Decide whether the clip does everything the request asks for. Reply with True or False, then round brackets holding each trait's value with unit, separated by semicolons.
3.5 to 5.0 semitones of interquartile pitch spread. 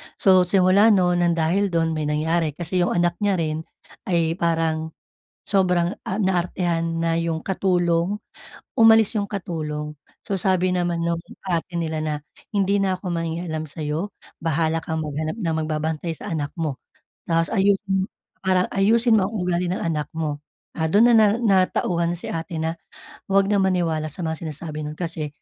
False (2.9 semitones)